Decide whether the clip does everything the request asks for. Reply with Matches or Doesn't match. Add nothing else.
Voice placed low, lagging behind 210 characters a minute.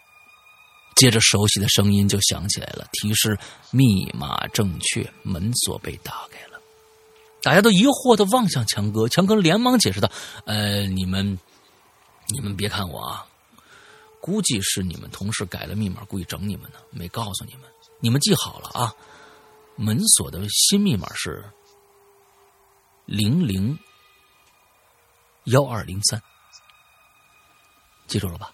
Matches